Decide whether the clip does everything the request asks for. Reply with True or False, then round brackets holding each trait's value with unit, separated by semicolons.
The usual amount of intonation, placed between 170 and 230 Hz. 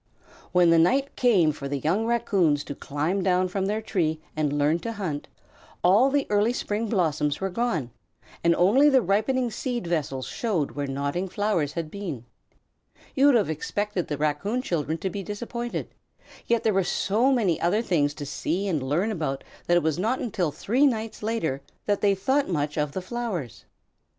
False (6.4 semitones; 185 Hz)